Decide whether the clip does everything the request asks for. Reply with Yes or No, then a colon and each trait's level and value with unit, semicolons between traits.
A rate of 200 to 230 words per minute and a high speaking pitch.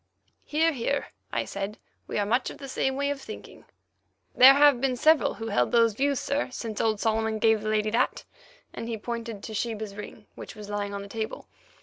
Yes: fast, 205 wpm; high, 225 Hz